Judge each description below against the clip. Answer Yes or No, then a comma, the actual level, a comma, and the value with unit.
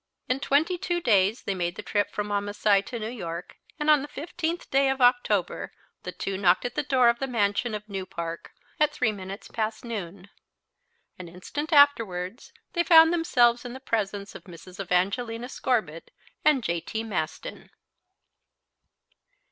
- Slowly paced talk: No, average, 165 wpm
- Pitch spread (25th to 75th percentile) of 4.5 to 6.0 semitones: Yes, wide, 5.6 semitones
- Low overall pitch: No, high, 220 Hz